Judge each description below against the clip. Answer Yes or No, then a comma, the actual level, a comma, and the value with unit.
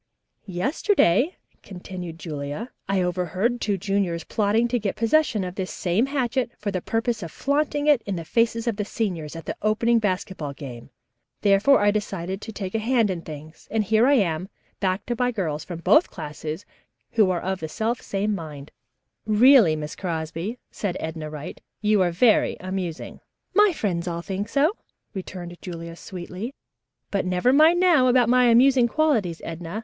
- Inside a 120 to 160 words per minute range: No, average, 170 wpm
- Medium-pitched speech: No, high, 200 Hz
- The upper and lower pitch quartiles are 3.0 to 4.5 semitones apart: No, wide, 5.5 semitones